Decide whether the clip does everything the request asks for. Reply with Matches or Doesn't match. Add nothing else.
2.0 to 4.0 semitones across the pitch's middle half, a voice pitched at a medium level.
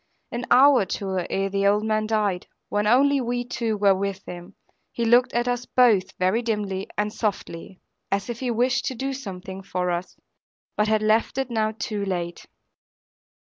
Doesn't match